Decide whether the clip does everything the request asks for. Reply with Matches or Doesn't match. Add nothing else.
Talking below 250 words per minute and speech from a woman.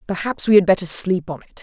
Doesn't match